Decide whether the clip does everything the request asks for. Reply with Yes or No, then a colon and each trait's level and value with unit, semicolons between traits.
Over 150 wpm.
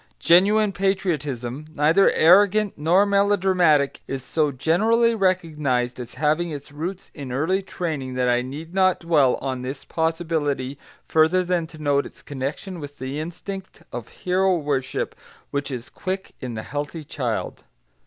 No: average, 145 wpm